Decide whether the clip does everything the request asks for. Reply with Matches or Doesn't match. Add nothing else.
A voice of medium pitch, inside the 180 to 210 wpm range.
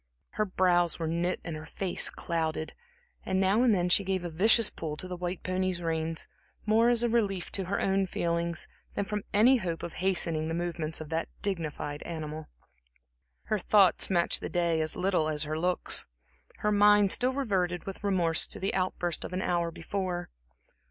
Matches